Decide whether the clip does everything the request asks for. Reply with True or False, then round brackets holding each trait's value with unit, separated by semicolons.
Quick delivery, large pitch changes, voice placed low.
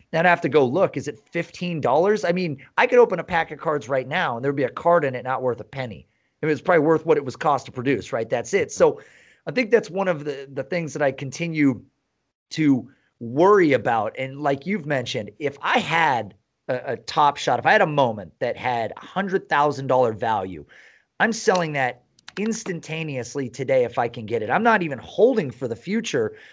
False (225 wpm; 6.2 semitones; 160 Hz)